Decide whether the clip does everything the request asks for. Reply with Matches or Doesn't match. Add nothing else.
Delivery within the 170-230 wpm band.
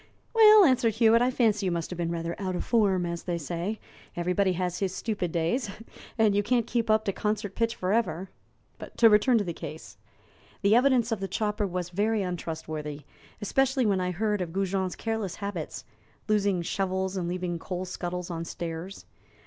Matches